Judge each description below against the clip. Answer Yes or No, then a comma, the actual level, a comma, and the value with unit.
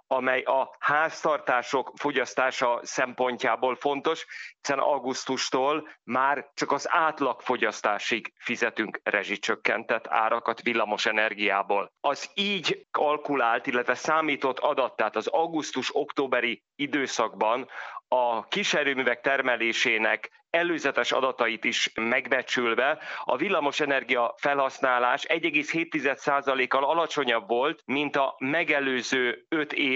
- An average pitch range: Yes, average, 3.1 semitones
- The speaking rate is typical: No, slow, 90 wpm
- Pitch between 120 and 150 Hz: Yes, low, 130 Hz